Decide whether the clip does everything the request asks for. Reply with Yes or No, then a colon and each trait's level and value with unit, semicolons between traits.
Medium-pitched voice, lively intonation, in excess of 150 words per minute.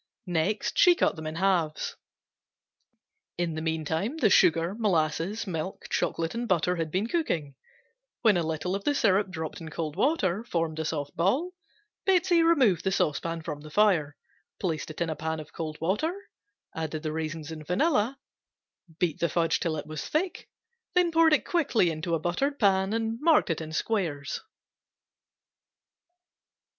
Yes: medium, 175 Hz; wide, 5.9 semitones; average, 160 wpm